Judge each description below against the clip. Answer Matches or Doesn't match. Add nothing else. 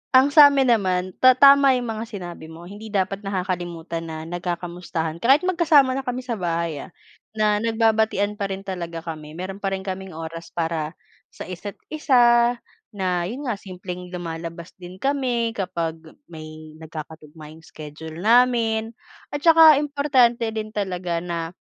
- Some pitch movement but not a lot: Doesn't match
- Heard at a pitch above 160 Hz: Matches